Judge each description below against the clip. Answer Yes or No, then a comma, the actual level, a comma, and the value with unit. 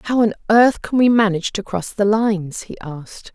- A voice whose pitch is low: No, high, 205 Hz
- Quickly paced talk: Yes, fast, 215 wpm